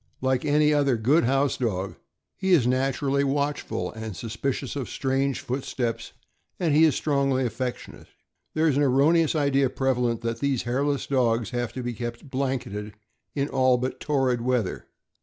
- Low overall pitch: Yes, low, 130 Hz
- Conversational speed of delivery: Yes, average, 160 wpm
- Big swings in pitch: No, average, 2.7 semitones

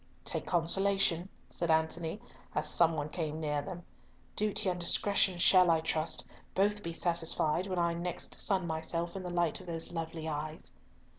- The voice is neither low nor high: Yes, medium, 170 Hz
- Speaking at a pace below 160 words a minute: No, average, 170 wpm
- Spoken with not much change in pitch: Yes, narrow, 2.3 semitones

